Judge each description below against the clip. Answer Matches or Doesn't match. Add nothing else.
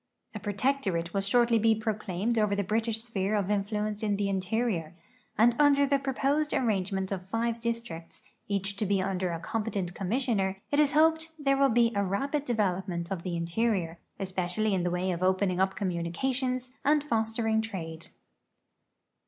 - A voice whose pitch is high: Matches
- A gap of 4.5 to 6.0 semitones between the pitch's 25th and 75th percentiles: Doesn't match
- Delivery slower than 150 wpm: Doesn't match